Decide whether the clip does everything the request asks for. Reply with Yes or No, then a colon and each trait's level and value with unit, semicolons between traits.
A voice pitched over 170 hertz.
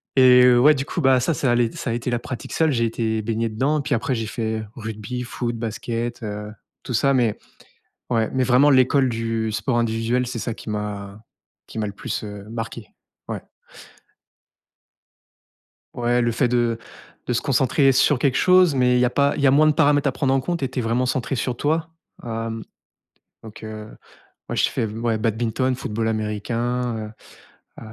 No: low, 120 Hz